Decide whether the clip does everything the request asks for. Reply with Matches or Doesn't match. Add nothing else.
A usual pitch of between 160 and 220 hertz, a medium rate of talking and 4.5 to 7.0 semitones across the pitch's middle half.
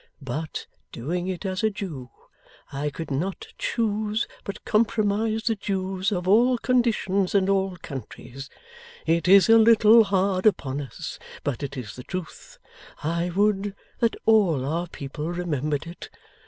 Matches